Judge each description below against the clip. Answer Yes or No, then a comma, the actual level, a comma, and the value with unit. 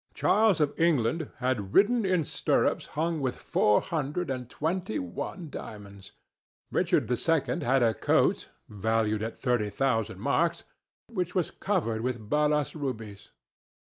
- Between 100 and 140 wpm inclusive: Yes, slow, 135 wpm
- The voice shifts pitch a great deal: Yes, wide, 7.0 semitones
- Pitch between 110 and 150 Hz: Yes, low, 135 Hz